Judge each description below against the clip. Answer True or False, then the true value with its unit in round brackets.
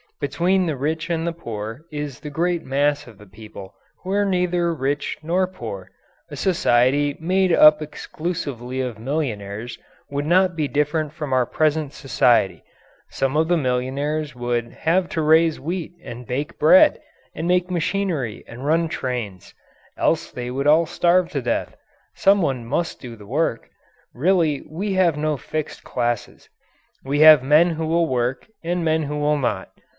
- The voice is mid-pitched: True (150 Hz)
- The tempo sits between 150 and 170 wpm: True (160 wpm)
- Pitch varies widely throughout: False (4.9 semitones)